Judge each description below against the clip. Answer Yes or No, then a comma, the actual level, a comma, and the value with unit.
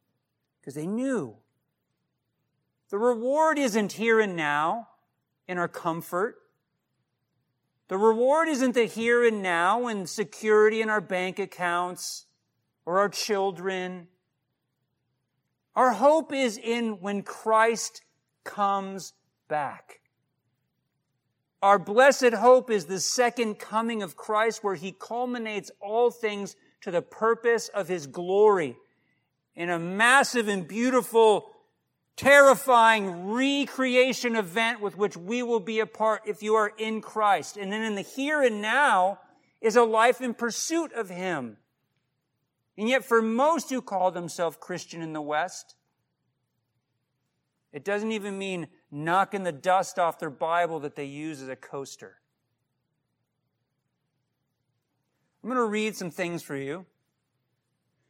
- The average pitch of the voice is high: Yes, high, 200 Hz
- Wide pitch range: Yes, wide, 6.4 semitones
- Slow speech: Yes, slow, 130 wpm